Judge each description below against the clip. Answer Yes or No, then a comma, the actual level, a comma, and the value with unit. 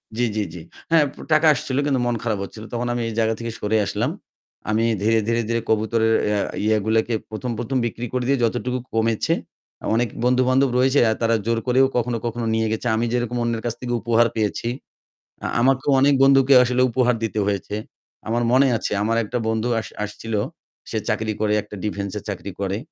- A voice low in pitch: Yes, low, 115 Hz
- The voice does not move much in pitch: Yes, narrow, 2.1 semitones